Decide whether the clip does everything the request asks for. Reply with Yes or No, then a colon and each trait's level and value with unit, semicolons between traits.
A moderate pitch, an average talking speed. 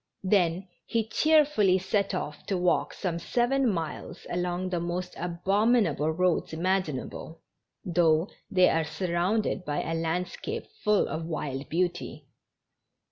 No: medium, 180 Hz; slow, 125 wpm